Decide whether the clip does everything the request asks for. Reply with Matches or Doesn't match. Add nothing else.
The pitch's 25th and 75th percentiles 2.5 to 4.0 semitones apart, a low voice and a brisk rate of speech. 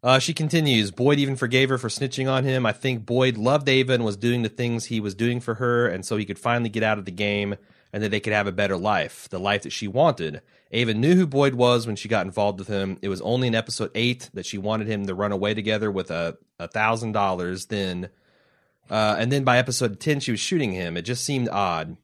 Matches